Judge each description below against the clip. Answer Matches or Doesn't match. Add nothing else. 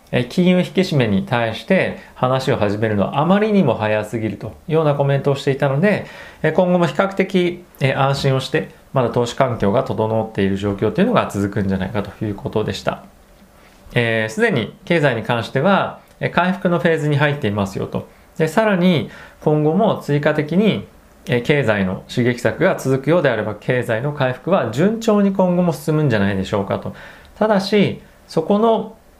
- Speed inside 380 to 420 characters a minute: Doesn't match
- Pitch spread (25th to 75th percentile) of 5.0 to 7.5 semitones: Doesn't match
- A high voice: Doesn't match